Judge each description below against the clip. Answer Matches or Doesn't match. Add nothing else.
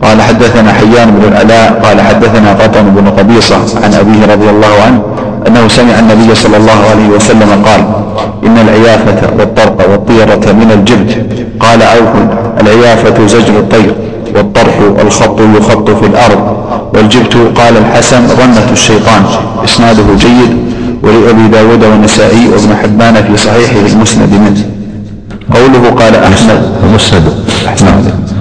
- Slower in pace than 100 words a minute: Doesn't match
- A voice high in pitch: Doesn't match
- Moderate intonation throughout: Doesn't match